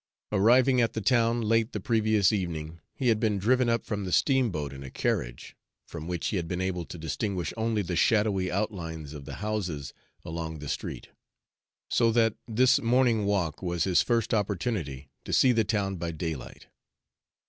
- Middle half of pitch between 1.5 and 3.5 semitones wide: No, wide, 5.5 semitones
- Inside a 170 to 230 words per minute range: Yes, average, 180 wpm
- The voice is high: No, low, 100 Hz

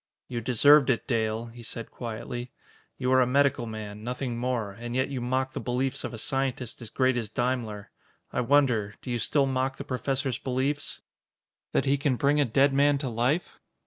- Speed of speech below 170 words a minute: No, average, 195 wpm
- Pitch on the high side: No, low, 125 Hz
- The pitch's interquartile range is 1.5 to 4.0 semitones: Yes, narrow, 2.5 semitones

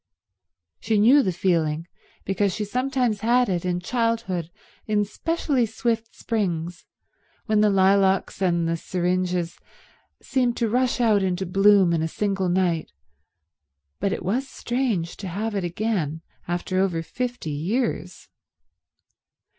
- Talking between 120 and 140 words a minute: Yes, slow, 135 wpm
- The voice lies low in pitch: No, high, 195 Hz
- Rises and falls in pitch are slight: No, average, 4.6 semitones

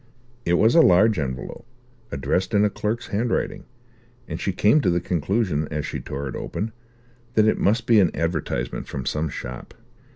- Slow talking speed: No, average, 175 wpm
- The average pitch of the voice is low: Yes, very low, 90 Hz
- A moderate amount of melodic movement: No, wide, 6.5 semitones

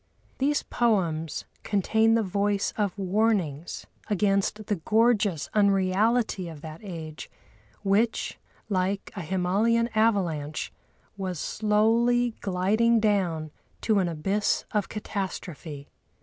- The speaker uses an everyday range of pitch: Yes, average, 3.4 semitones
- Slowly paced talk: Yes, slow, 105 wpm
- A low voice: No, high, 200 Hz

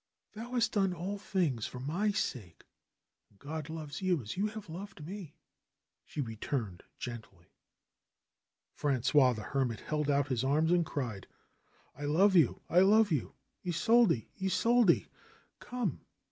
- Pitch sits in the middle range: Yes, medium, 160 Hz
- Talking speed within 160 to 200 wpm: No, average, 145 wpm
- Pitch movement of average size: No, wide, 7.0 semitones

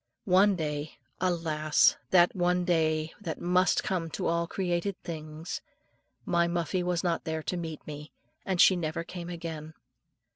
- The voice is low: No, medium, 170 Hz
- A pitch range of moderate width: No, narrow, 2.1 semitones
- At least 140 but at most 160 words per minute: Yes, average, 150 wpm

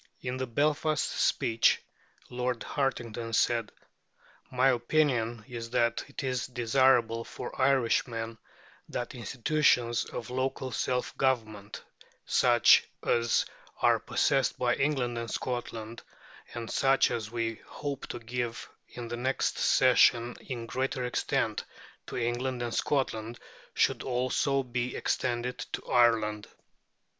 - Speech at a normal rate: No, slow, 120 wpm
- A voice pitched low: Yes, low, 120 Hz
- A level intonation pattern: Yes, narrow, 2.0 semitones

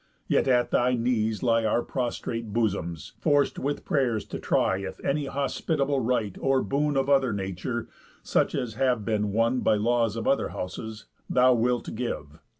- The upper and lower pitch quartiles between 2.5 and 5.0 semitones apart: Yes, average, 3.5 semitones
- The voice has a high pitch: No, low, 120 Hz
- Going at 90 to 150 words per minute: No, average, 165 wpm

